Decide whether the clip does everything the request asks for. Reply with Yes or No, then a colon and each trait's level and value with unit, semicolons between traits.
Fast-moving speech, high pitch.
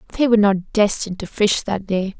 Yes: fast, 220 wpm; high, 205 Hz